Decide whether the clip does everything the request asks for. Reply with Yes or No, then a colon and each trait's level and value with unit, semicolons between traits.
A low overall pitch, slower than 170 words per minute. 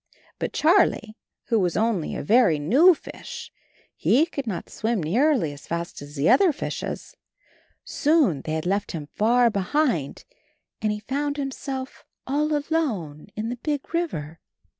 No: high, 230 Hz; average, 150 wpm